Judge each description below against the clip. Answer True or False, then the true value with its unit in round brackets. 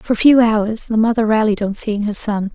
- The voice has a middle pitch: False (220 Hz)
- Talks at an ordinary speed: False (260 wpm)